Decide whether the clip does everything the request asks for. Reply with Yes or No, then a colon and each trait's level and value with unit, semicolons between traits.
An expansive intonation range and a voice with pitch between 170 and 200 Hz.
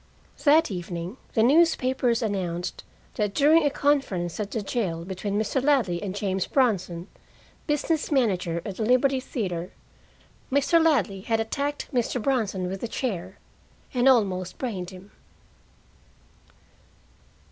No: wide, 6.3 semitones; high, 220 Hz